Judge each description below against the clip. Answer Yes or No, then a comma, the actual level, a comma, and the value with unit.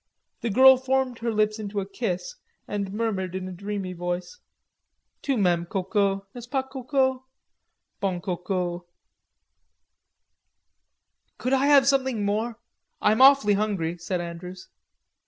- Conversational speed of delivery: No, slow, 130 wpm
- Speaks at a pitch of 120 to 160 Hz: No, high, 210 Hz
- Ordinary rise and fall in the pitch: No, wide, 5.7 semitones